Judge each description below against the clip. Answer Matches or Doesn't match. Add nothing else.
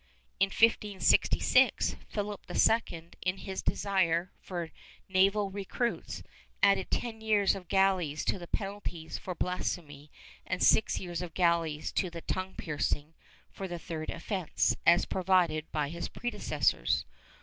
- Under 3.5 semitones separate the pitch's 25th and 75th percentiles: Matches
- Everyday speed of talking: Doesn't match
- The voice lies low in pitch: Doesn't match